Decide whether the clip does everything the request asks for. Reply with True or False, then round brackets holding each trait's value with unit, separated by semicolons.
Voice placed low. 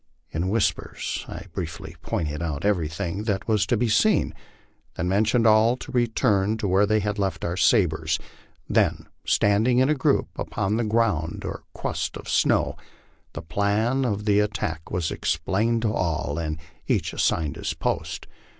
True (105 Hz)